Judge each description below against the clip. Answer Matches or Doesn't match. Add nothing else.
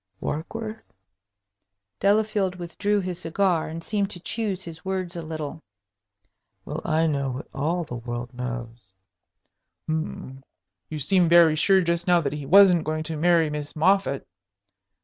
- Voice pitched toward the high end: Doesn't match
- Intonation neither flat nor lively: Matches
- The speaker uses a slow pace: Doesn't match